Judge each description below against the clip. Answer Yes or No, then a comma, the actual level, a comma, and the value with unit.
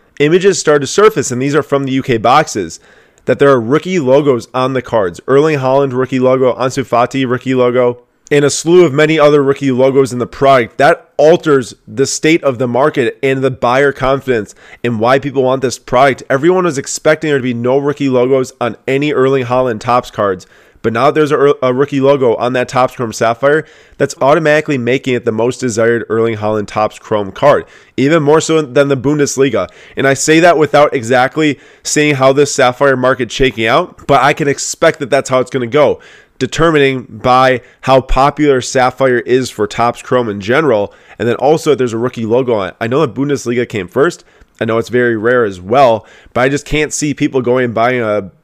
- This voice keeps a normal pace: No, fast, 210 wpm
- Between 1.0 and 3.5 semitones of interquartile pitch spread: Yes, average, 2.8 semitones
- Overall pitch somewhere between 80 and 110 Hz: No, low, 130 Hz